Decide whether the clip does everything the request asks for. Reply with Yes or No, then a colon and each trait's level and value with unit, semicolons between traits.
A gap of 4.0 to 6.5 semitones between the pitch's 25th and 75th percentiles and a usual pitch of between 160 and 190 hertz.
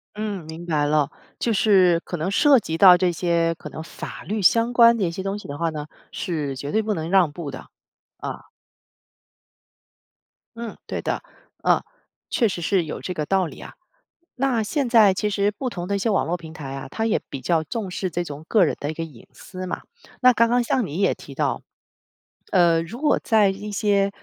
Yes: average, 4.8 semitones; medium, 185 Hz